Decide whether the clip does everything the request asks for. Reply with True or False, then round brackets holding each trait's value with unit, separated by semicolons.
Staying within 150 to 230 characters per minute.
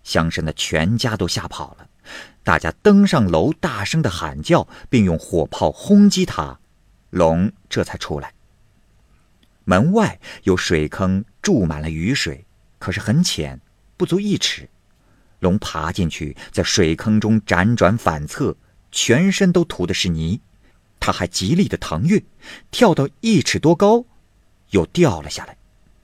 True (200 characters per minute)